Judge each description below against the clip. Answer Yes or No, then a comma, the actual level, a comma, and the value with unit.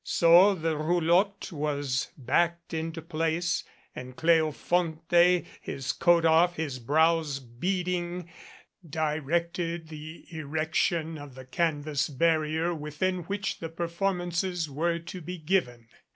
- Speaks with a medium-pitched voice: Yes, medium, 165 Hz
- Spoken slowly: Yes, slow, 110 wpm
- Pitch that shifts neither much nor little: No, narrow, 2.2 semitones